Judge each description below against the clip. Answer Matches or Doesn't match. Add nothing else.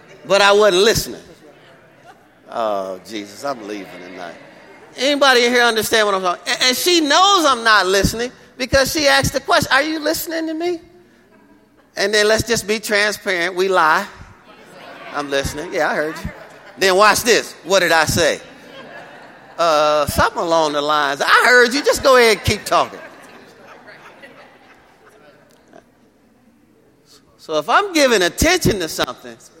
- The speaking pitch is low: Doesn't match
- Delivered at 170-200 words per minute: Doesn't match